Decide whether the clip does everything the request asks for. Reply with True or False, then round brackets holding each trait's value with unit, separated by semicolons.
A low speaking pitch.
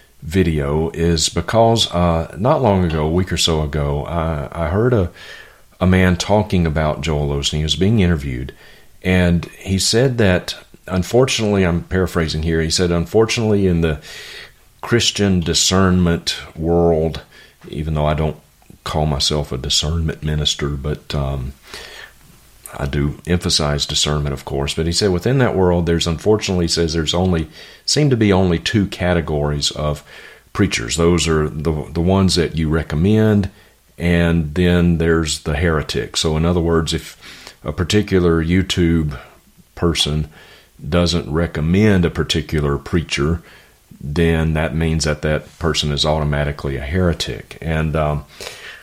True (85 Hz)